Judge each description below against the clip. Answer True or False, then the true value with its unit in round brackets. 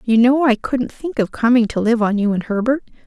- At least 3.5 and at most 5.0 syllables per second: False (5.3 syllables/s)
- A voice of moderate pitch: False (235 Hz)